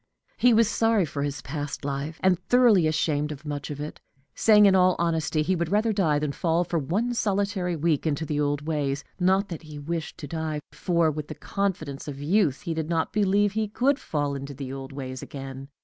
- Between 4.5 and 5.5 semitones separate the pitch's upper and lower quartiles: Yes, average, 4.8 semitones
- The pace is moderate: No, fast, 210 wpm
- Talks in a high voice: No, medium, 160 Hz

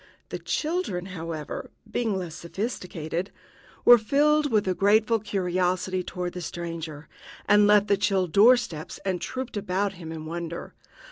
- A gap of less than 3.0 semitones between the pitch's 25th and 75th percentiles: No, average, 3.8 semitones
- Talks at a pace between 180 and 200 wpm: No, average, 145 wpm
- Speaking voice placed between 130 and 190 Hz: Yes, medium, 185 Hz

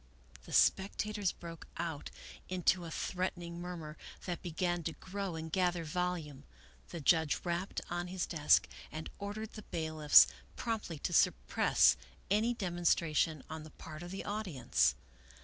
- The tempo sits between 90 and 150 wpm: Yes, average, 140 wpm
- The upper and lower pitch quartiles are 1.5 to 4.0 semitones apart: Yes, average, 2.8 semitones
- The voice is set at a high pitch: No, medium, 175 Hz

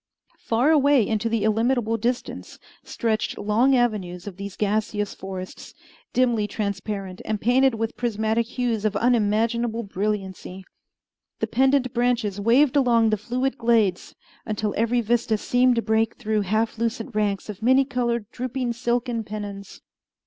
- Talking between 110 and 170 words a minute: Yes, average, 140 wpm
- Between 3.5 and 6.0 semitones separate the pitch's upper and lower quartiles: No, average, 2.7 semitones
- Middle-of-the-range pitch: No, high, 225 Hz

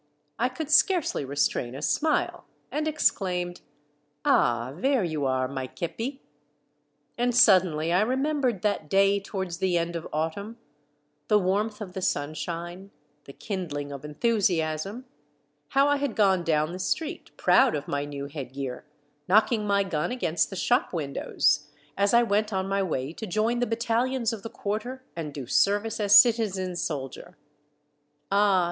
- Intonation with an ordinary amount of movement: No, wide, 6.8 semitones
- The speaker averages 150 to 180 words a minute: Yes, average, 160 wpm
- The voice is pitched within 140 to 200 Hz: Yes, high, 190 Hz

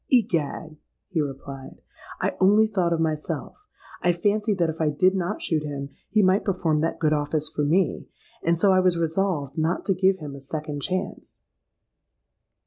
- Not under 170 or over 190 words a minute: Yes, average, 175 wpm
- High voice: No, medium, 165 Hz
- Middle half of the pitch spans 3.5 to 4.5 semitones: Yes, average, 3.8 semitones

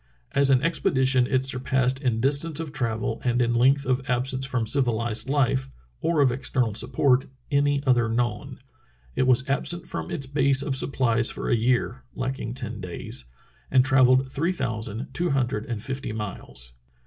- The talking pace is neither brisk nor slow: Yes, average, 165 wpm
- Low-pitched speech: Yes, low, 130 Hz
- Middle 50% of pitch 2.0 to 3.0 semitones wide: Yes, narrow, 2.5 semitones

